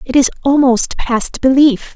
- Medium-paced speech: Yes, average, 155 wpm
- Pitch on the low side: No, very high, 260 Hz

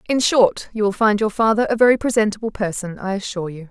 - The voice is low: No, high, 210 Hz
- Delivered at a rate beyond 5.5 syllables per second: Yes, 6.4 syllables/s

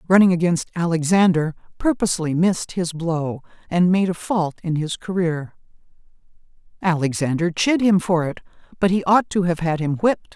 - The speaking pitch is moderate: Yes, medium, 175 Hz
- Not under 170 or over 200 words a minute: No, average, 155 wpm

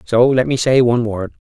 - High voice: No, low, 120 Hz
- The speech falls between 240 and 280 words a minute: Yes, fast, 250 wpm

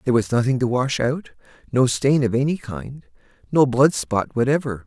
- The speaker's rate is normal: Yes, average, 160 wpm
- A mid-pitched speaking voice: No, low, 125 Hz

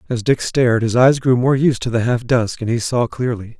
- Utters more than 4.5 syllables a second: Yes, 5.3 syllables/s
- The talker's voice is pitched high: No, low, 120 Hz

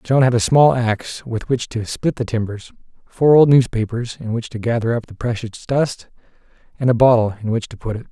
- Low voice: Yes, low, 120 Hz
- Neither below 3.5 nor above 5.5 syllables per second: Yes, 5.4 syllables/s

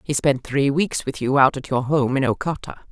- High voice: No, low, 135 Hz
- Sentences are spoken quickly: Yes, fast, 245 wpm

